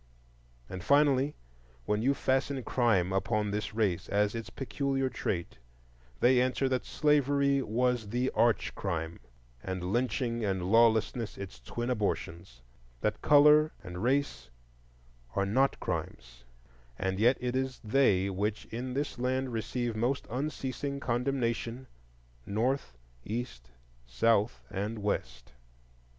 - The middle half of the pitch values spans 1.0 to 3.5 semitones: No, average, 4.8 semitones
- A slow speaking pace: Yes, slow, 120 wpm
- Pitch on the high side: No, low, 115 Hz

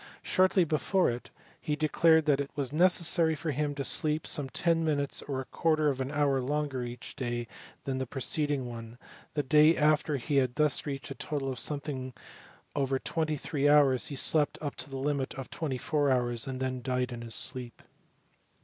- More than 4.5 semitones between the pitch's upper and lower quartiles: No, average, 2.7 semitones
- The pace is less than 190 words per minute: No, average, 195 wpm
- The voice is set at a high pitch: No, medium, 140 Hz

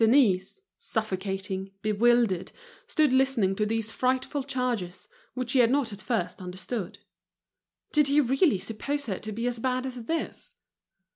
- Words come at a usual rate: Yes, average, 145 wpm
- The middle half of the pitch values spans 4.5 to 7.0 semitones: Yes, average, 4.8 semitones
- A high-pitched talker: Yes, high, 235 Hz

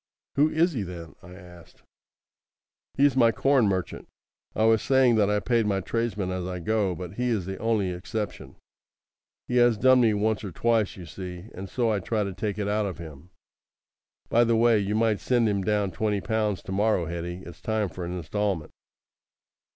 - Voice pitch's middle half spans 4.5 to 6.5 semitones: No, average, 3.7 semitones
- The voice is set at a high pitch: No, low, 105 Hz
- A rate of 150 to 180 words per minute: No, average, 195 wpm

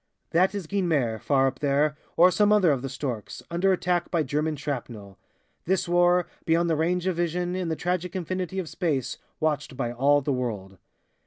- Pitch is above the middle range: No, medium, 160 Hz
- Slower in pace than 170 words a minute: No, average, 185 wpm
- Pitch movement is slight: No, average, 4.8 semitones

